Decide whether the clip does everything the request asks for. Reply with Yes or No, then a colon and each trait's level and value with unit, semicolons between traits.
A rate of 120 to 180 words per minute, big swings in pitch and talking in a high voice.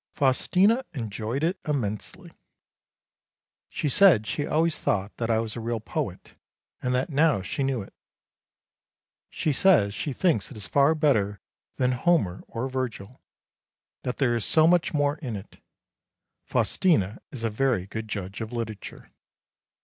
No: average, 150 wpm; wide, 5.7 semitones; low, 125 Hz